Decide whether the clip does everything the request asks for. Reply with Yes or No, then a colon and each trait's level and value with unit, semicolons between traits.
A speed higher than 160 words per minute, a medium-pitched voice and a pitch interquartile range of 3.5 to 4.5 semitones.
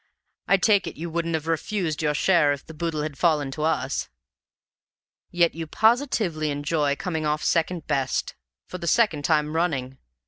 No: average, 170 wpm; medium, 160 Hz; narrow, 2.5 semitones